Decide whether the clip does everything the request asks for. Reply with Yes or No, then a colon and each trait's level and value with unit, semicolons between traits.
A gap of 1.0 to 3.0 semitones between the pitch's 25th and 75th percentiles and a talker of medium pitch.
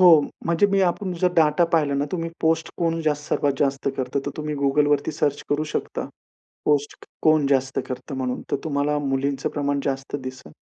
Yes: narrow, 2.6 semitones; medium, 145 Hz